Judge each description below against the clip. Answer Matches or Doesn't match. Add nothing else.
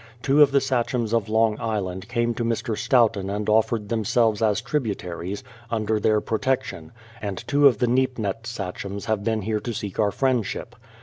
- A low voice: Matches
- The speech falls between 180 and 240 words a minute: Matches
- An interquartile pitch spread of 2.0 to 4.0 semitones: Matches